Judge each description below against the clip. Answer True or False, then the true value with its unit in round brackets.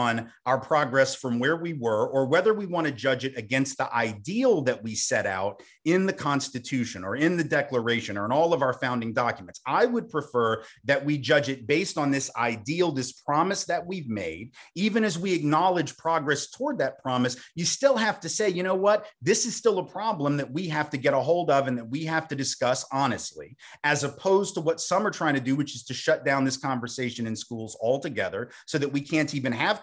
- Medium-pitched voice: True (145 Hz)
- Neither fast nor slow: False (225 wpm)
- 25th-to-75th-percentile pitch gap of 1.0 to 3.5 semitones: False (4.9 semitones)